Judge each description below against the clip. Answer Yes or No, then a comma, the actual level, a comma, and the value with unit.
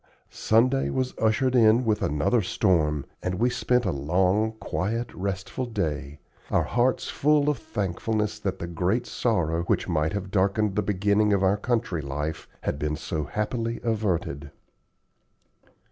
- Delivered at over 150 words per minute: No, average, 145 wpm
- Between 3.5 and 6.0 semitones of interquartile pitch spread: Yes, average, 5.0 semitones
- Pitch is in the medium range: No, low, 100 Hz